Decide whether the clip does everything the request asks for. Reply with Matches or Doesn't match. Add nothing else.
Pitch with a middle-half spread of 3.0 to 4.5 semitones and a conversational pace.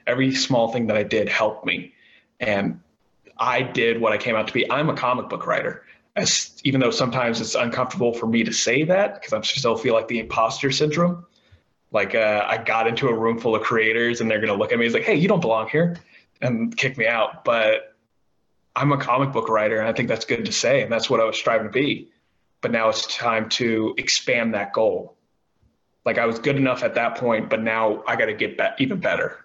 Doesn't match